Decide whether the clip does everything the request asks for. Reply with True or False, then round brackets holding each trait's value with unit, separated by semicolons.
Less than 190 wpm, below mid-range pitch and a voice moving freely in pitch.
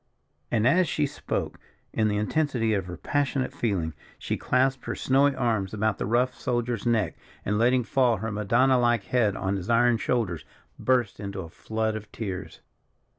False (175 wpm; 115 Hz; 3.5 semitones)